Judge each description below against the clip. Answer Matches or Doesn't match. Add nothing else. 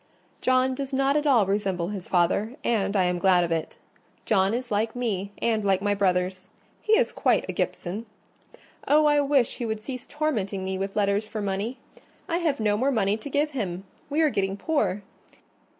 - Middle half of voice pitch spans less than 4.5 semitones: Doesn't match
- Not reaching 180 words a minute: Doesn't match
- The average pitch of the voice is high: Matches